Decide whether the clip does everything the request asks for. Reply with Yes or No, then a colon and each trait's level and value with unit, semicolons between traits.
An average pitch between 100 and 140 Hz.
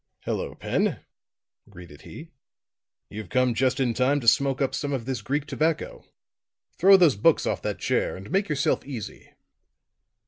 Yes: low, 135 Hz